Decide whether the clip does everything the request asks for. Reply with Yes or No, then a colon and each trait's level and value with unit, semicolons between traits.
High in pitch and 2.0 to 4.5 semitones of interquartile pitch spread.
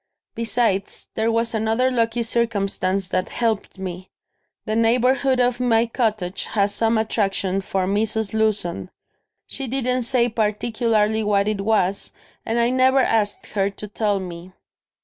Yes: high, 220 Hz; average, 2.9 semitones